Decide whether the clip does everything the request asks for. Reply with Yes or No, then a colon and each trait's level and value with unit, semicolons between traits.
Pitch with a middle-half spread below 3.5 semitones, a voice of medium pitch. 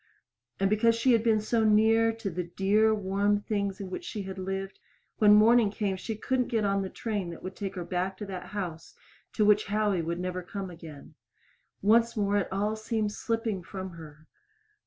No: narrow, 2.5 semitones; high, 205 Hz